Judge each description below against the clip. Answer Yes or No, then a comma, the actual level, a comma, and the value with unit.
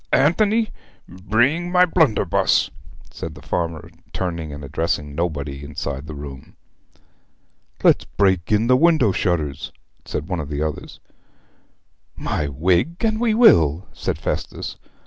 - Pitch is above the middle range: No, very low, 85 Hz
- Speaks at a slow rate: Yes, slow, 125 wpm